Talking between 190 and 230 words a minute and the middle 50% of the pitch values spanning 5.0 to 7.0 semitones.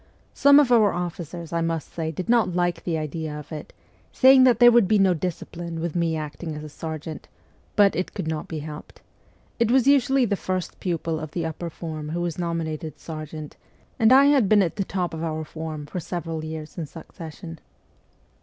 No: average, 200 wpm; average, 3.6 semitones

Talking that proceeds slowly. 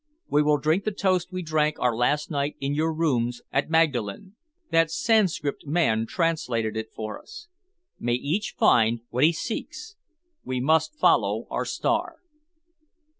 No: average, 150 wpm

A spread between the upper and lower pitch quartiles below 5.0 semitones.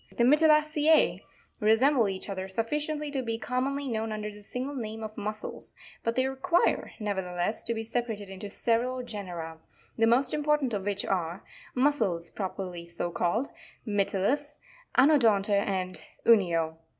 No: average, 5.3 semitones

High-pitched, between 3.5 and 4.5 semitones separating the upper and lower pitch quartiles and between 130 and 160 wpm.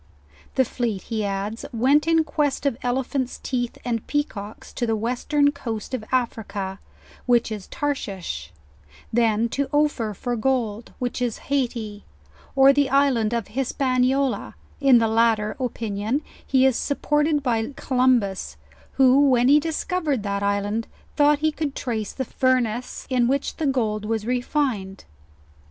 Yes: high, 245 Hz; average, 4.0 semitones; average, 145 wpm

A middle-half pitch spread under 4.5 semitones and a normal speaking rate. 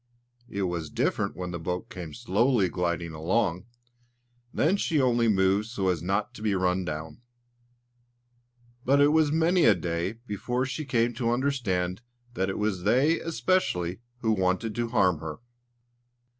No: average, 5.3 semitones; average, 155 wpm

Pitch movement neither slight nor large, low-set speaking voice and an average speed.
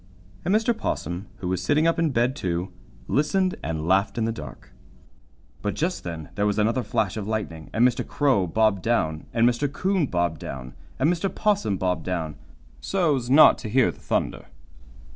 No: wide, 8.4 semitones; low, 110 Hz; average, 180 wpm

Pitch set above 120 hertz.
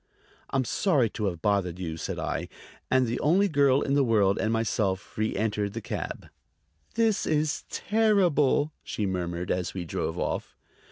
No: low, 115 Hz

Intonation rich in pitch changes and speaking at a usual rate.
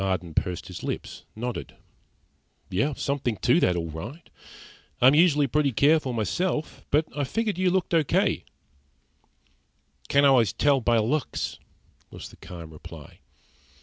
No: wide, 6.1 semitones; slow, 130 wpm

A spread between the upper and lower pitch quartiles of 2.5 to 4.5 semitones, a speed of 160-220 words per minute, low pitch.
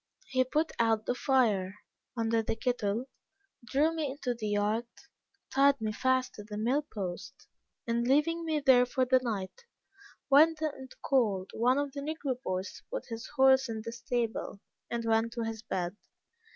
No: average, 3.6 semitones; average, 170 wpm; high, 245 Hz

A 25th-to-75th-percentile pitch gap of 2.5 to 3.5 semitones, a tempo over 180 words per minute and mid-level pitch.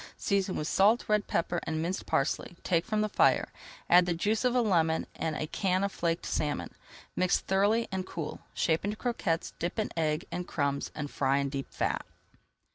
No: average, 4.2 semitones; average, 195 wpm; medium, 175 Hz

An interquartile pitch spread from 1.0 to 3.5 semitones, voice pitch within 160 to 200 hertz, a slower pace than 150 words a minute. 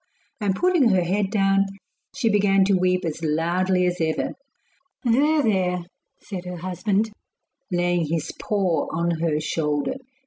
Yes: average, 3.2 semitones; medium, 185 Hz; average, 140 wpm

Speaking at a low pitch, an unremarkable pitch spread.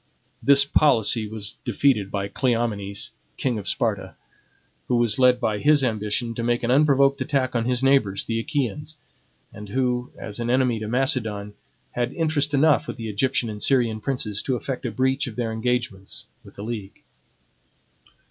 Yes: low, 120 Hz; average, 3.7 semitones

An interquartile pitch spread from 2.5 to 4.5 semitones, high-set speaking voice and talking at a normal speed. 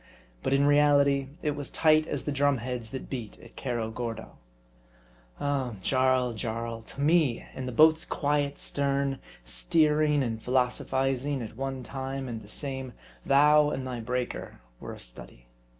No: average, 3.0 semitones; low, 135 Hz; average, 155 wpm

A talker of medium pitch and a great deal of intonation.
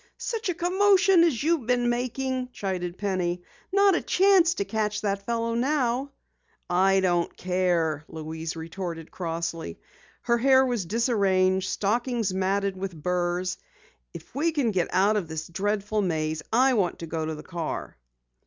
No: high, 200 Hz; wide, 6.1 semitones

